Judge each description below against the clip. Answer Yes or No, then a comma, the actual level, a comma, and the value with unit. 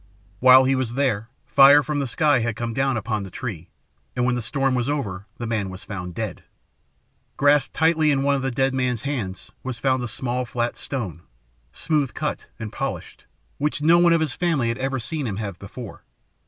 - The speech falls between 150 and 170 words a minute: No, fast, 205 wpm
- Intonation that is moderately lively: Yes, average, 4.0 semitones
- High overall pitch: No, low, 130 Hz